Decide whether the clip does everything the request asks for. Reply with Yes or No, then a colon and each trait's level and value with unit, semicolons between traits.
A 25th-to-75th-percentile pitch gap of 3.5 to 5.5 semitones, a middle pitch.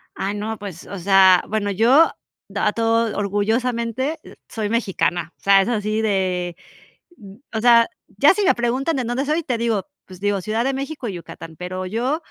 No: average, 3.9 semitones; high, 220 Hz